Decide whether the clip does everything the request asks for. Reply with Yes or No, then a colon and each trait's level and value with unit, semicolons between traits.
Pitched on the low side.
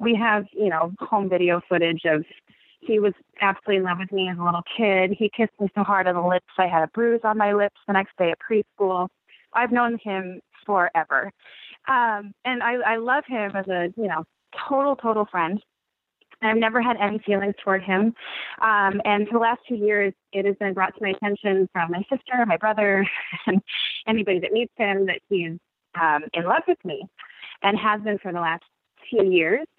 No: high, 205 Hz